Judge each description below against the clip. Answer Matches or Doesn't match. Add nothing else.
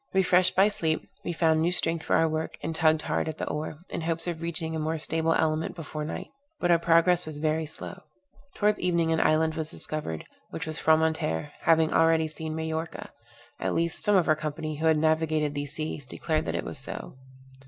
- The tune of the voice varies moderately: Doesn't match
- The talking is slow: Doesn't match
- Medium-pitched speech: Matches